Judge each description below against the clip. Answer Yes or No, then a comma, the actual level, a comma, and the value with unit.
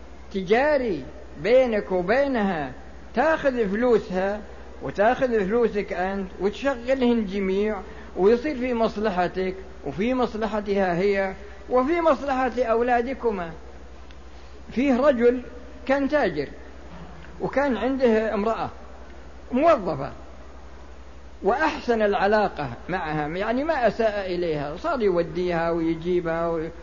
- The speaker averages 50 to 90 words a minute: Yes, average, 85 wpm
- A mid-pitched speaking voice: No, high, 205 Hz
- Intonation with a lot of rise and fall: Yes, wide, 6.4 semitones